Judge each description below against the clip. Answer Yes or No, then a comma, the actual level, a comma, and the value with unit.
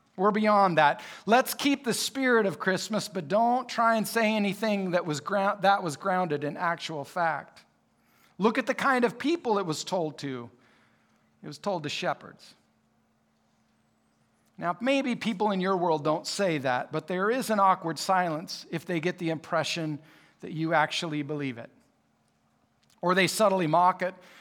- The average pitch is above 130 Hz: Yes, medium, 185 Hz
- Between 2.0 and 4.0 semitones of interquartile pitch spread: No, average, 5.0 semitones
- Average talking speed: Yes, average, 170 wpm